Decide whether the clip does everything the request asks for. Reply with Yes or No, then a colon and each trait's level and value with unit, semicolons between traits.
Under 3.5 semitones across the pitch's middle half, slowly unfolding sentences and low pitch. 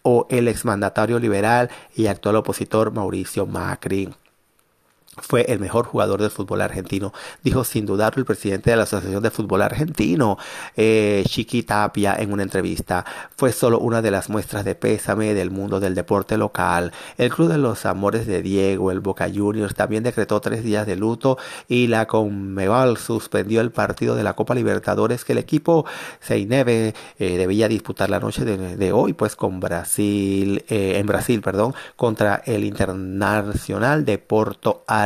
No: average, 2.7 semitones; average, 165 wpm; low, 105 Hz